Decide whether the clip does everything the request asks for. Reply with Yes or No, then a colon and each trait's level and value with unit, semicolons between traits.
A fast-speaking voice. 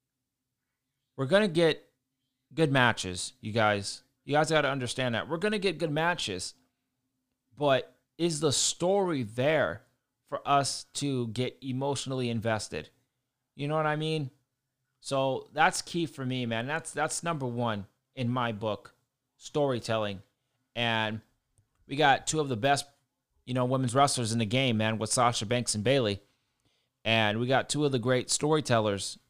No: average, 155 wpm